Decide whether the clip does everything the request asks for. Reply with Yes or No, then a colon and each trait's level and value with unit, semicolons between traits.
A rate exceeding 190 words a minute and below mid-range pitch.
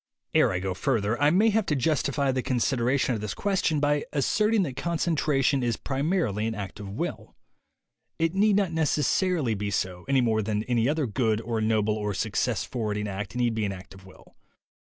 Yes: average, 200 wpm; low, 125 Hz